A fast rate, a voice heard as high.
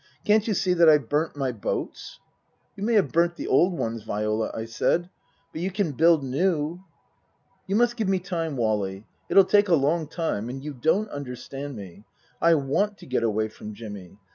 No: fast, 210 wpm; medium, 150 Hz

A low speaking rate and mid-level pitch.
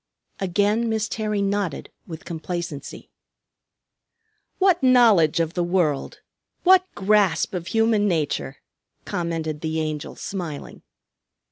Yes: slow, 105 wpm; medium, 180 Hz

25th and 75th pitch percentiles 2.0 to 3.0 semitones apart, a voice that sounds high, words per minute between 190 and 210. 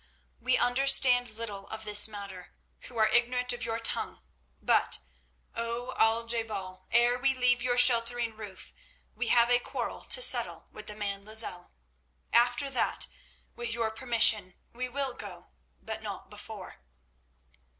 No: narrow, 2.4 semitones; high, 230 Hz; average, 150 wpm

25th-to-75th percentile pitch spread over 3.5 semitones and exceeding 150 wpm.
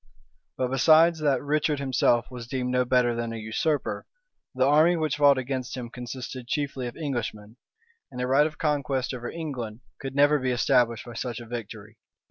No: average, 3.1 semitones; average, 180 wpm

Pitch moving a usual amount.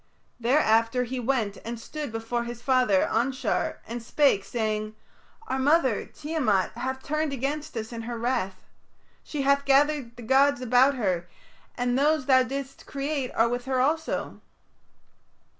Yes: average, 3.3 semitones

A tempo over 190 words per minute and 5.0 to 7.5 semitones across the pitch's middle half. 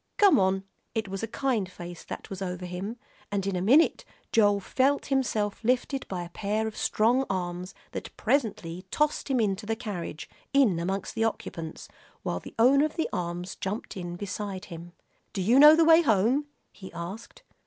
No: average, 185 wpm; average, 5.3 semitones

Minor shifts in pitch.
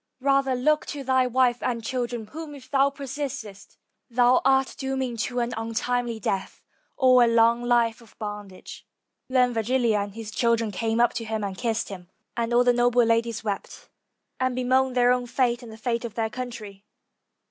Yes: narrow, 2.2 semitones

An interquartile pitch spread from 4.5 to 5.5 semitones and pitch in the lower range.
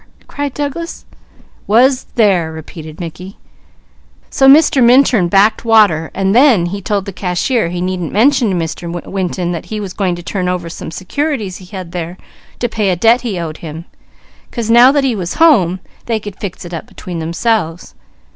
No: average, 5.2 semitones; high, 195 Hz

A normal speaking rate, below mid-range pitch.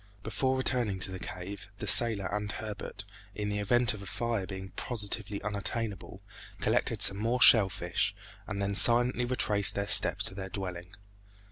Yes: average, 160 wpm; low, 100 Hz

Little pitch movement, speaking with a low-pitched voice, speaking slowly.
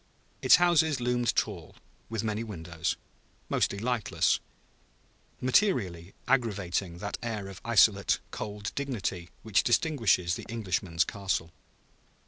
No: average, 4.8 semitones; low, 105 Hz; slow, 110 wpm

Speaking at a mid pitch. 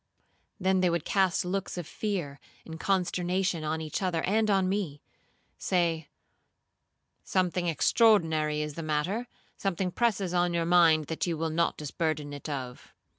Yes: medium, 170 Hz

